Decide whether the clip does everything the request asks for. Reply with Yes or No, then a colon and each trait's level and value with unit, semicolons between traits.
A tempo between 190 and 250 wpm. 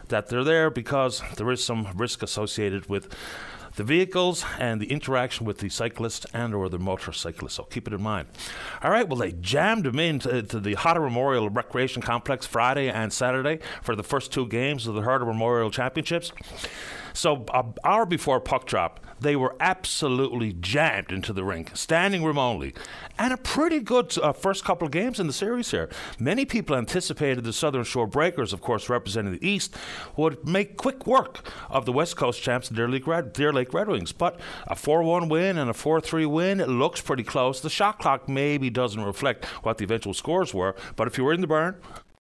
Yes: average, 195 wpm